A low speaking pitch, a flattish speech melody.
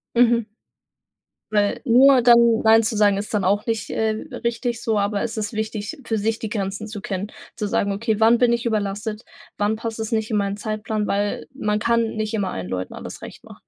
No: high, 215 Hz; narrow, 1.9 semitones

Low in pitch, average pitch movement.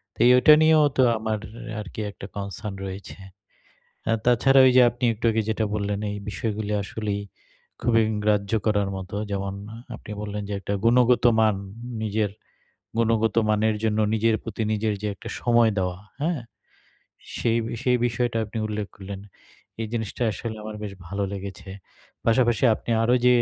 No: low, 110 Hz; narrow, 2.2 semitones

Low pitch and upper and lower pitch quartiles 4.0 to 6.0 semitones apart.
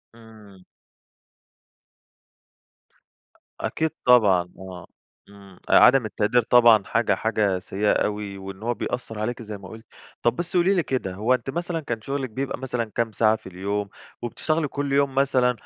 Yes: low, 115 Hz; average, 4.4 semitones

